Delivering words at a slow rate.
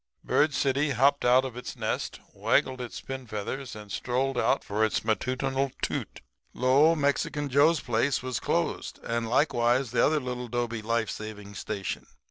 No: average, 160 wpm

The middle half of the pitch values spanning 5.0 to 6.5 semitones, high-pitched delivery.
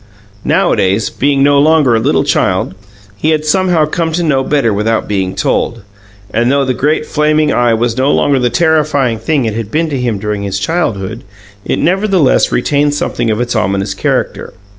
No: wide, 5.4 semitones; low, 130 Hz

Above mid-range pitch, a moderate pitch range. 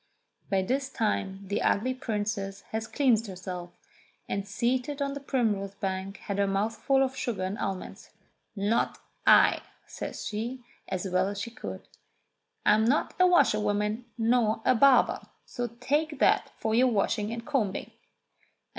Yes: high, 220 Hz; average, 4.2 semitones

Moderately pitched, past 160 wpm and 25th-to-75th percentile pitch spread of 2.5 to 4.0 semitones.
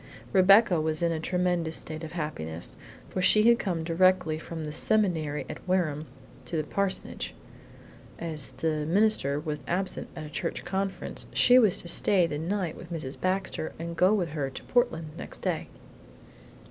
Yes: medium, 170 Hz; average, 170 wpm; average, 3.3 semitones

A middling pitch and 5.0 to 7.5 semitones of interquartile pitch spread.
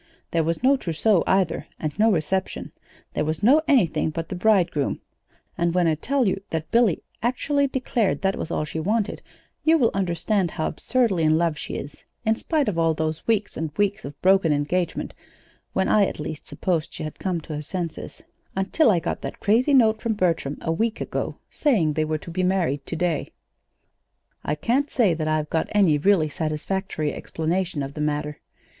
Yes: medium, 175 Hz; average, 5.3 semitones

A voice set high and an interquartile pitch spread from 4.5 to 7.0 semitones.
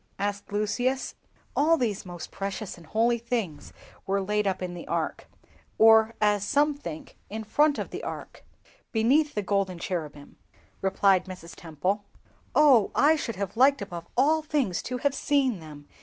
Yes: high, 210 Hz; wide, 5.6 semitones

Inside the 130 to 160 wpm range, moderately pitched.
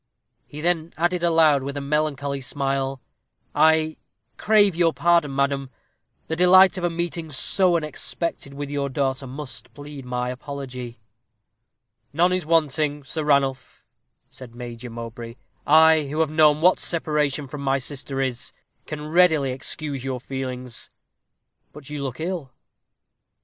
Yes: average, 140 wpm; medium, 145 Hz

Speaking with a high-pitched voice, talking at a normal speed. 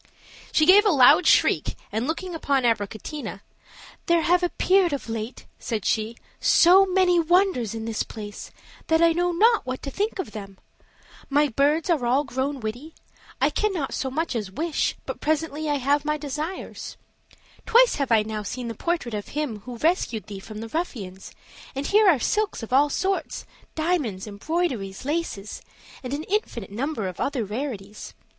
Yes: very high, 285 Hz; average, 170 wpm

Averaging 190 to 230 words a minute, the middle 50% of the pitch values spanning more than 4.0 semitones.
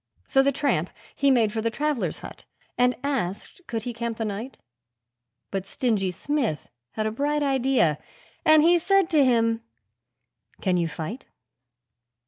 No: average, 150 wpm; average, 4.6 semitones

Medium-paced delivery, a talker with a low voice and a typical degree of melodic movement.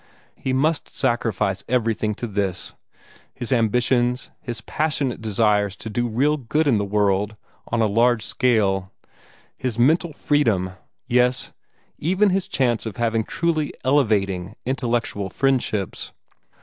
No: slow, 125 wpm; low, 120 Hz; average, 4.1 semitones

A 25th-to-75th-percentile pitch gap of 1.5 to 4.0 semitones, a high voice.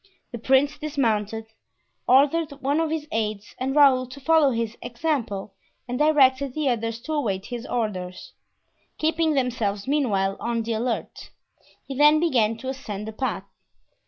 No: average, 4.7 semitones; very high, 255 Hz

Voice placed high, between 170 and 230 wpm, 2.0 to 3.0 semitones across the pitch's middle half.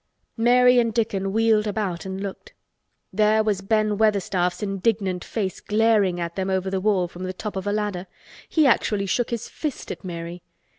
Yes: high, 205 Hz; average, 180 wpm; narrow, 2.6 semitones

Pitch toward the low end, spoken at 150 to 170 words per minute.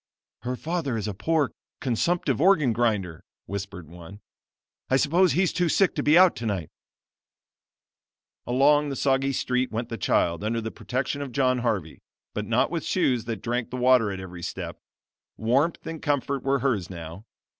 Yes: low, 125 Hz; average, 165 wpm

